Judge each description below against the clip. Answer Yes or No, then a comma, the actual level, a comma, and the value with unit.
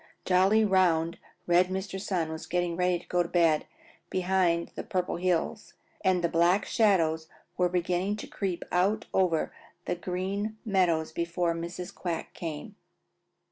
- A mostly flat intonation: Yes, narrow, 1.9 semitones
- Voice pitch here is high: No, medium, 180 Hz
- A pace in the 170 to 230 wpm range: No, average, 145 wpm